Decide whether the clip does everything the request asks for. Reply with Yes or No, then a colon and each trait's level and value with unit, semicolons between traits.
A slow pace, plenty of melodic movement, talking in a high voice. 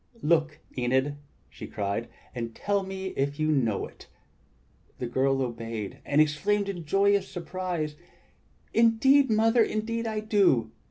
No: slow, 130 wpm; wide, 7.6 semitones; medium, 160 Hz